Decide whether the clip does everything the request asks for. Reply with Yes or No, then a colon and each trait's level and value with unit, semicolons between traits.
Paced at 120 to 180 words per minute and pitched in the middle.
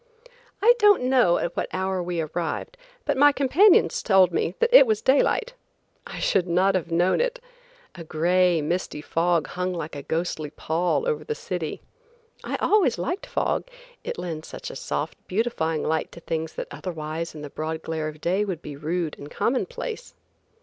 Yes: average, 175 wpm; medium, 175 Hz